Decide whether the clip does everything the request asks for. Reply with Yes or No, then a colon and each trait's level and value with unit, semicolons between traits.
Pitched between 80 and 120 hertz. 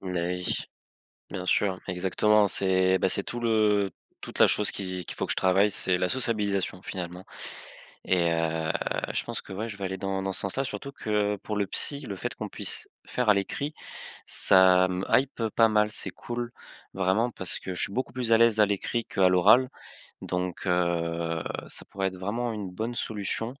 Yes: low, 100 Hz